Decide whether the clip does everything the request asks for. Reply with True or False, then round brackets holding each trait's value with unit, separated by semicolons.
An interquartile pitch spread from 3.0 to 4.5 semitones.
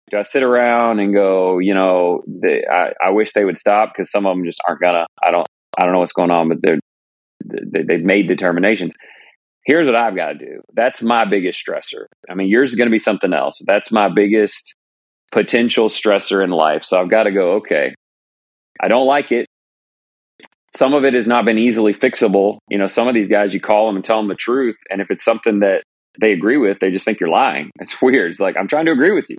True (3.6 semitones)